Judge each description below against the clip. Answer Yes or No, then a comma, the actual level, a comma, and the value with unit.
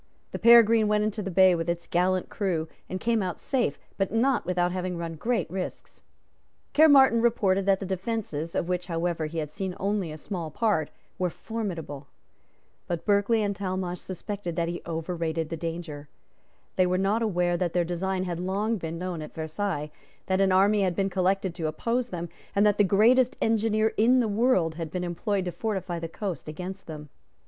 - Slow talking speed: No, average, 190 wpm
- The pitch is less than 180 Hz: No, medium, 185 Hz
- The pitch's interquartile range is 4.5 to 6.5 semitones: No, average, 3.6 semitones